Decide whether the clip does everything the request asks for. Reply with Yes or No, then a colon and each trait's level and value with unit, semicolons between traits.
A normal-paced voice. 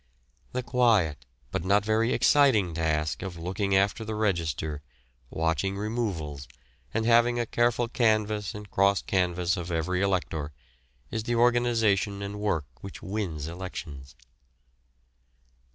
No: slow, 125 wpm